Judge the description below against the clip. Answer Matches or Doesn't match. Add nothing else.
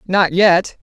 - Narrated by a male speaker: Doesn't match